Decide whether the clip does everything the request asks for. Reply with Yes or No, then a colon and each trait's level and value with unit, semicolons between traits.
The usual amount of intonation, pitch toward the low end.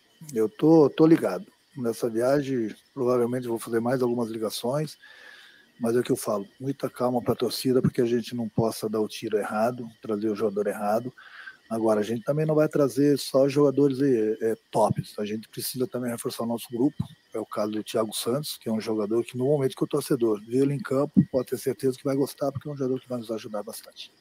Yes: average, 3.8 semitones; low, 125 Hz